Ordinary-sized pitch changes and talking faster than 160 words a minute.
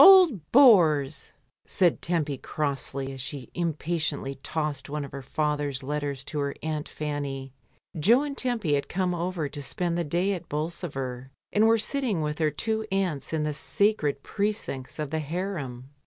Yes: average, 4.5 semitones; average, 170 wpm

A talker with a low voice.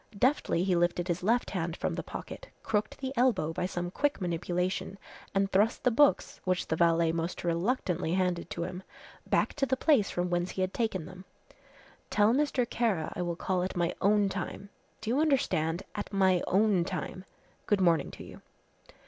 No: medium, 185 Hz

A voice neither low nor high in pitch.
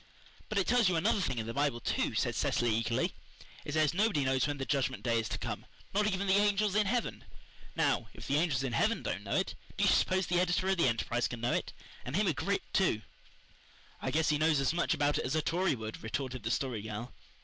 Yes: medium, 150 Hz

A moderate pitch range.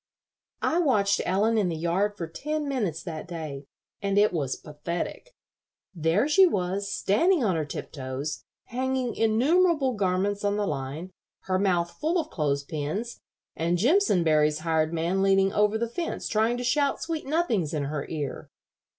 No: wide, 7.1 semitones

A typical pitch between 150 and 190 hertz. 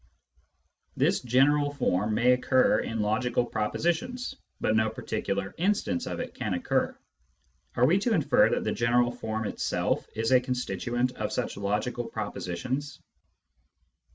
No: low, 120 Hz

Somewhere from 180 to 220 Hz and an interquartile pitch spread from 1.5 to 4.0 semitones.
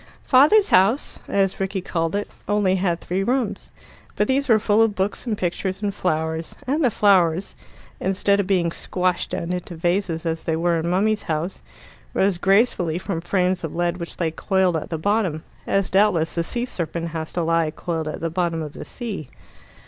Yes: medium, 185 Hz; average, 3.4 semitones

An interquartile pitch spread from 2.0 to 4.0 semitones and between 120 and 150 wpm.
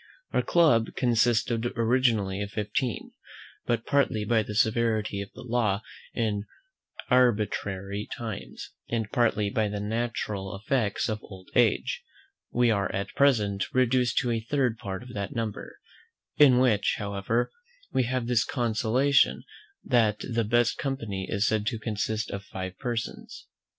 Yes: average, 2.9 semitones; average, 140 wpm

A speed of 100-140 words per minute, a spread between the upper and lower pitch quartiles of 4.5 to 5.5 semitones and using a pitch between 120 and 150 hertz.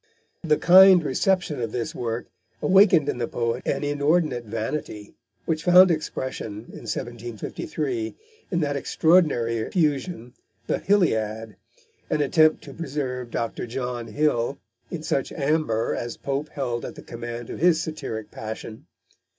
Yes: slow, 135 wpm; average, 5.1 semitones; low, 135 Hz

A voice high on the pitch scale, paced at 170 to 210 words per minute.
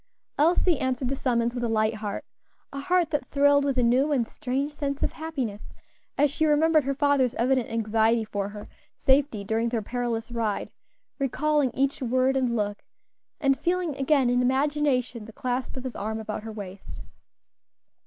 Yes: very high, 255 Hz; average, 175 wpm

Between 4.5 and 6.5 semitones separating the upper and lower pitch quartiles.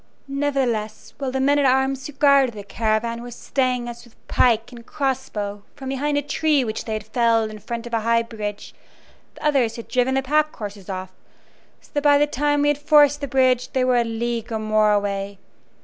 No: average, 3.9 semitones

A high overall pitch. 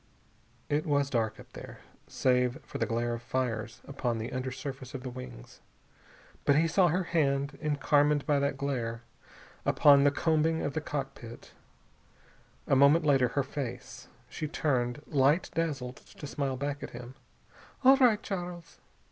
No: medium, 140 Hz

